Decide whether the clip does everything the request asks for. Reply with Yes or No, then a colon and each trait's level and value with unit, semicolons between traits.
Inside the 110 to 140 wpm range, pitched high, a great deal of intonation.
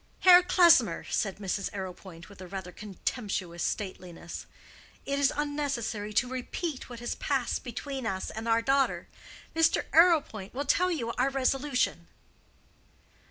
Yes: slow, 135 wpm; high, 240 Hz; wide, 6.2 semitones